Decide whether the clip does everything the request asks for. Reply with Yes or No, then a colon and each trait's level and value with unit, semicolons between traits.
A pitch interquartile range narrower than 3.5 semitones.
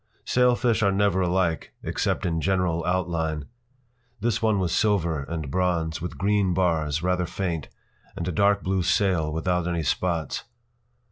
Yes: average, 2.9 semitones